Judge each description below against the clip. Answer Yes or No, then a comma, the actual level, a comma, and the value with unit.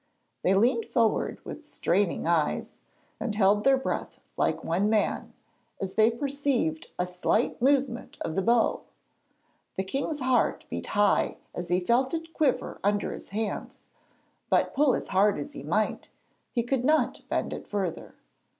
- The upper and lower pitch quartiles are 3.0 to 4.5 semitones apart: No, wide, 5.4 semitones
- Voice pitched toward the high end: Yes, high, 220 Hz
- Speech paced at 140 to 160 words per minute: Yes, average, 155 wpm